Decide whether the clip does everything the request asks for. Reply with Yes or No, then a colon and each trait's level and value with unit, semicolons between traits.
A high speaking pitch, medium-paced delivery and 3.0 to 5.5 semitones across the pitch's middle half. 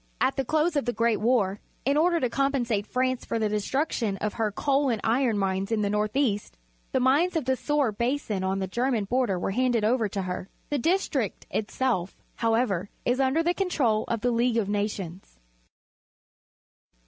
Yes: high, 235 Hz; average, 185 wpm; average, 4.4 semitones